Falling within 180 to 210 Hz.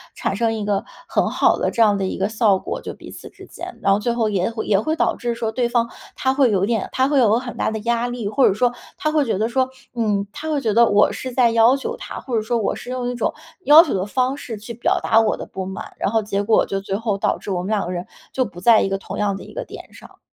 No: high, 225 Hz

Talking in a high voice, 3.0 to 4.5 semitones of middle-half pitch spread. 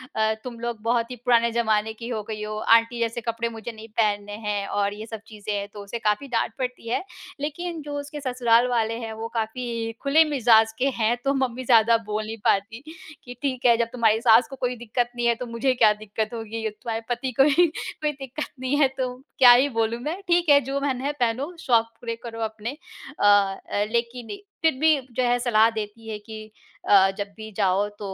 No: high, 230 Hz; narrow, 2.5 semitones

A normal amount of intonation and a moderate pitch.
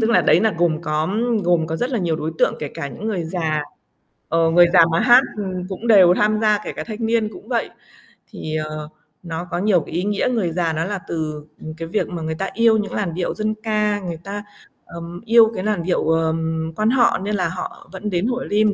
Yes: average, 4.6 semitones; medium, 180 Hz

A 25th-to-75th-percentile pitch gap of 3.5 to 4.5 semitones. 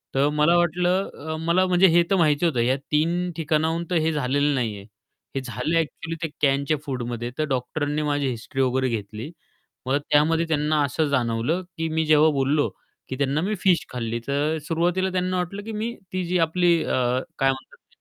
Yes: average, 4.1 semitones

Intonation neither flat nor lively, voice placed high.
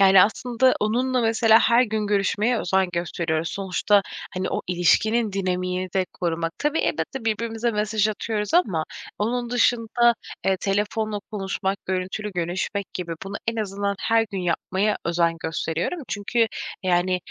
Yes: average, 3.6 semitones; high, 205 Hz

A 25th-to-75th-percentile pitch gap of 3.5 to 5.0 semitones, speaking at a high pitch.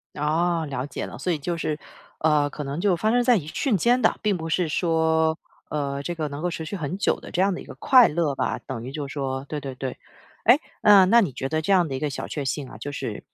No: average, 4.1 semitones; medium, 160 Hz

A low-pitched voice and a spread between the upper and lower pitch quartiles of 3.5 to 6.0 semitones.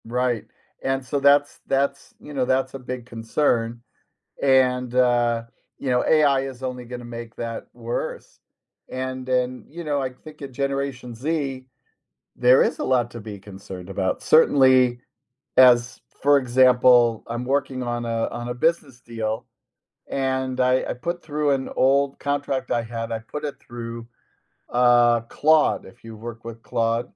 No: low, 125 Hz; narrow, 2.6 semitones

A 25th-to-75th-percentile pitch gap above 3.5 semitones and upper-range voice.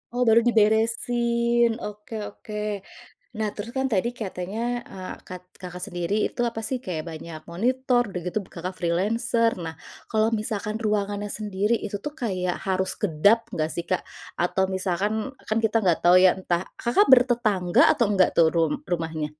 Yes: average, 4.1 semitones; high, 210 Hz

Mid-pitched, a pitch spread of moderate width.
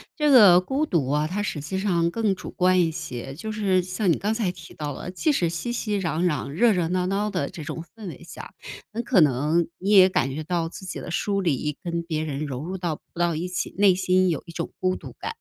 Yes: medium, 180 Hz; average, 3.5 semitones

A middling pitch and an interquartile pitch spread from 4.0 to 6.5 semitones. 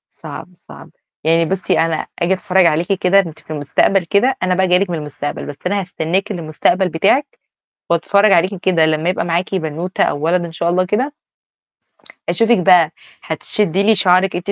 No: medium, 180 Hz; average, 2.9 semitones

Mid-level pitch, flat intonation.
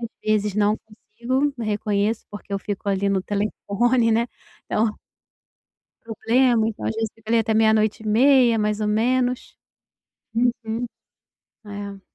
No: high, 220 Hz; narrow, 2.0 semitones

